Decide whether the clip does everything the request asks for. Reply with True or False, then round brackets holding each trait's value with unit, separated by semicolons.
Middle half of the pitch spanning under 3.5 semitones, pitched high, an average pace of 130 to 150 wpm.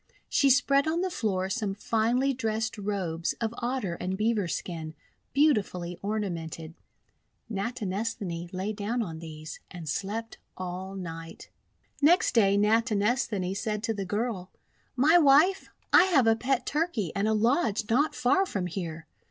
False (5.2 semitones; 210 Hz; 145 wpm)